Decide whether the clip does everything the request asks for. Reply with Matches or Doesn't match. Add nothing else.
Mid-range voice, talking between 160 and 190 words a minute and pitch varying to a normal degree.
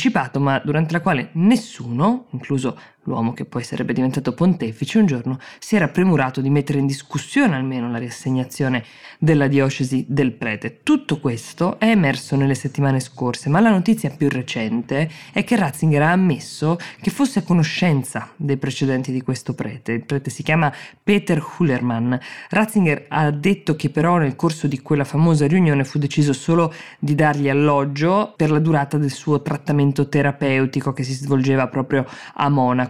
Matches